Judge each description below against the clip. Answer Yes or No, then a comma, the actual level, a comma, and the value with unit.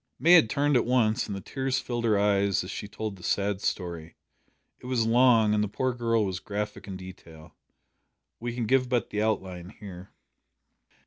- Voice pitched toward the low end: Yes, low, 105 Hz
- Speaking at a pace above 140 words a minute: Yes, average, 190 wpm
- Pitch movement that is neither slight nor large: Yes, average, 3.8 semitones